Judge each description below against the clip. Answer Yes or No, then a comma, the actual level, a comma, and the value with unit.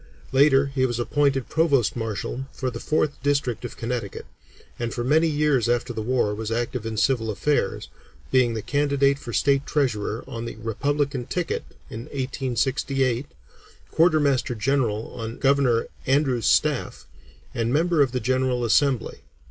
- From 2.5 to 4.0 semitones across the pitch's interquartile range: Yes, average, 3.3 semitones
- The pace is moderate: Yes, average, 150 wpm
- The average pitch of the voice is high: No, low, 130 Hz